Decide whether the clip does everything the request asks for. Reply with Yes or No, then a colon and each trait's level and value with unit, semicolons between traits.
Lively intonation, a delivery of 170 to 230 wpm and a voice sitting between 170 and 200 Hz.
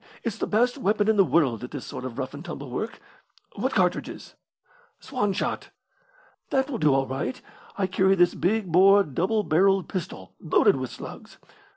Yes: wide, 6.8 semitones; average, 180 wpm; medium, 185 Hz